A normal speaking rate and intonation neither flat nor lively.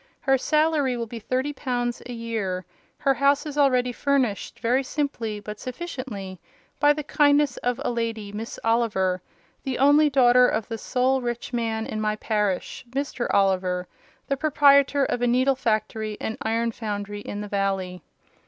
Yes: average, 160 wpm; average, 4.3 semitones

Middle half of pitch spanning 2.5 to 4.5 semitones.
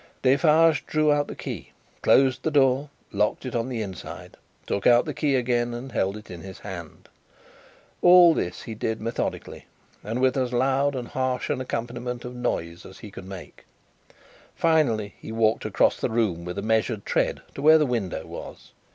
Yes: average, 4.0 semitones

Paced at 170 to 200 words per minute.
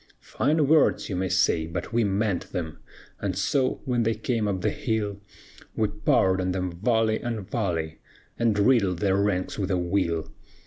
Yes: average, 175 wpm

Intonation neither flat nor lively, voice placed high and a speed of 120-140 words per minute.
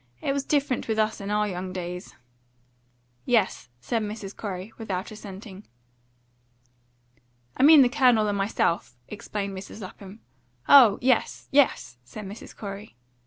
Yes: average, 3.0 semitones; high, 210 Hz; slow, 135 wpm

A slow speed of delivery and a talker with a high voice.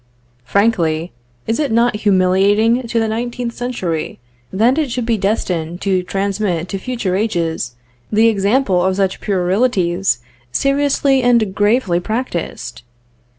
Yes: slow, 125 wpm; high, 205 Hz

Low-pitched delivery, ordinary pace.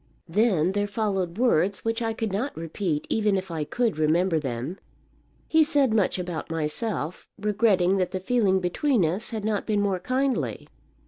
No: high, 195 Hz; average, 170 wpm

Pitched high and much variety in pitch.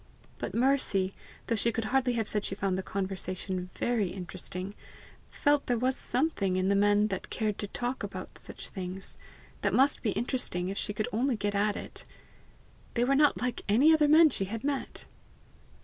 No: high, 215 Hz; average, 4.6 semitones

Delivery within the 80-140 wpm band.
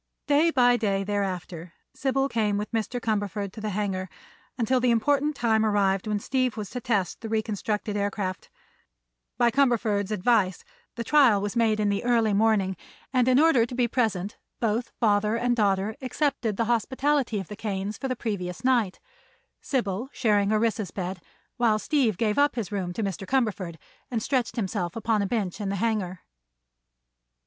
No: average, 170 wpm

